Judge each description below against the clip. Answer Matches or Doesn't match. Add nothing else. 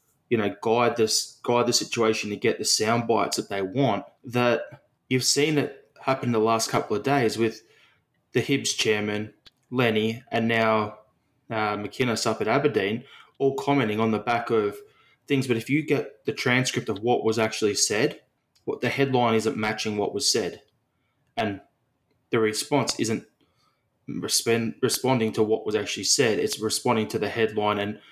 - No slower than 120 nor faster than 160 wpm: Doesn't match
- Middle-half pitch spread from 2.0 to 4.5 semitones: Matches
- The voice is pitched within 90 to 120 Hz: Matches